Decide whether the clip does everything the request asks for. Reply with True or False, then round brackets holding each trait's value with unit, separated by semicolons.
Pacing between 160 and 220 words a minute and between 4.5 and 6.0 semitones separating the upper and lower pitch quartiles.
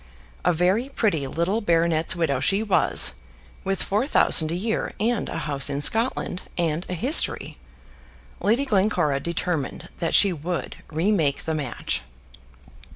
False (140 wpm; 4.8 semitones)